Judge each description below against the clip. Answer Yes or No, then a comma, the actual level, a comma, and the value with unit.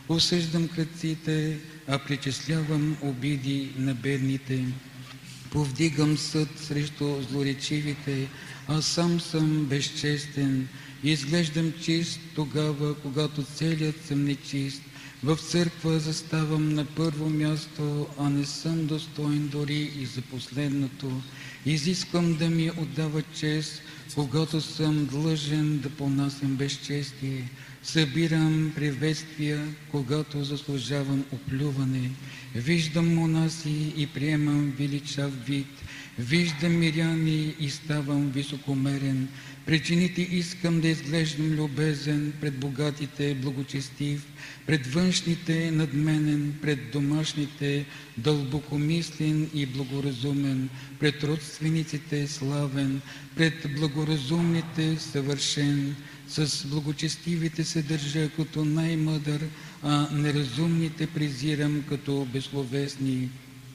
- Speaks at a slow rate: Yes, slow, 90 wpm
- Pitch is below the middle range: No, medium, 150 Hz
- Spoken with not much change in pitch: Yes, narrow, 1.9 semitones